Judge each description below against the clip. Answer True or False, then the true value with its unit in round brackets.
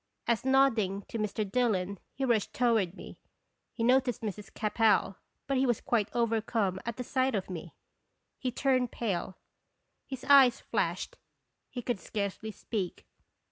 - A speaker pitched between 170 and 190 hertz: False (225 Hz)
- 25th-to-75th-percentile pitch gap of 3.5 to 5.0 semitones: True (3.8 semitones)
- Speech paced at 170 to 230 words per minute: False (150 wpm)